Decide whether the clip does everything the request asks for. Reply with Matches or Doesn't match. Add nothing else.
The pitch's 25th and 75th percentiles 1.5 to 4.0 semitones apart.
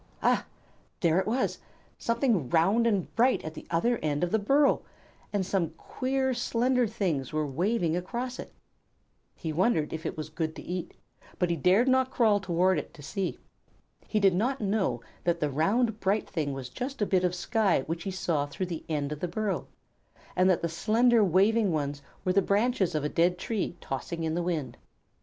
Doesn't match